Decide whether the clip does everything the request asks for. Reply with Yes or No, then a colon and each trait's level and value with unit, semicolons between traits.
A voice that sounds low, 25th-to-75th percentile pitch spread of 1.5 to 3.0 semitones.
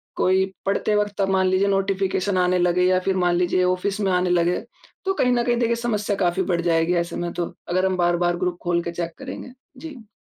No: medium, 185 Hz; narrow, 2.4 semitones